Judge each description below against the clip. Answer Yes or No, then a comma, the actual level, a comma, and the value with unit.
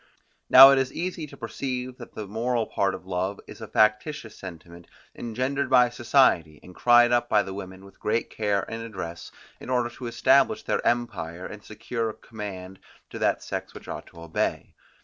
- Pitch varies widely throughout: No, average, 4.8 semitones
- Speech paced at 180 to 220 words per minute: Yes, average, 185 wpm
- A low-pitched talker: Yes, low, 115 Hz